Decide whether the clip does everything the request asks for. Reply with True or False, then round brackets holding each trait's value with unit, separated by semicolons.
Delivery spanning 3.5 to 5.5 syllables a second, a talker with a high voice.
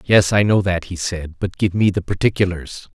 False (5.0 syllables/s; 95 Hz)